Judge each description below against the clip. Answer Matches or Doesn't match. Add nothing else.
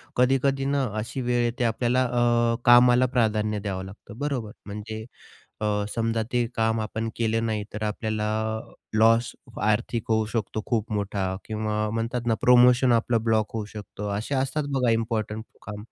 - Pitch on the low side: Matches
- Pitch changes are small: Matches